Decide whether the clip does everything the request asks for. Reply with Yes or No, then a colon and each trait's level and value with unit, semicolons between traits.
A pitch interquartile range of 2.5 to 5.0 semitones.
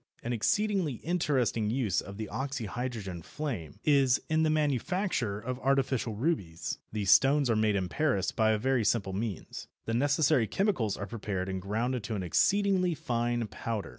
No: wide, 5.6 semitones